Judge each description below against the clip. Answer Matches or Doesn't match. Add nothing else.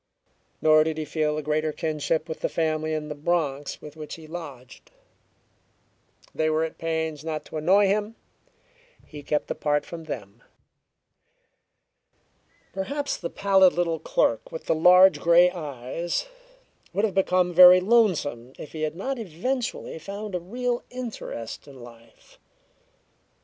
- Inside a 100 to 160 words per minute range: Matches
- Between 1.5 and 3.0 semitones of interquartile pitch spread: Doesn't match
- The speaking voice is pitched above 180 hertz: Doesn't match